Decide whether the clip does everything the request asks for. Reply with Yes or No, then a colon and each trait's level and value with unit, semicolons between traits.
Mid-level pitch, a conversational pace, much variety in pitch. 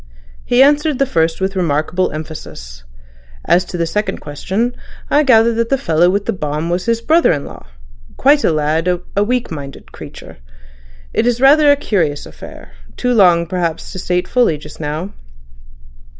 Yes: medium, 180 Hz; average, 160 wpm; wide, 7.3 semitones